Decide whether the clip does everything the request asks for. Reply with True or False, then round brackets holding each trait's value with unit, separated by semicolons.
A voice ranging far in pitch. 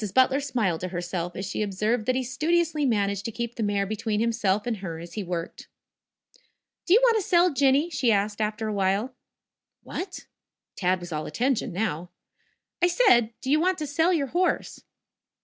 True (6.4 semitones)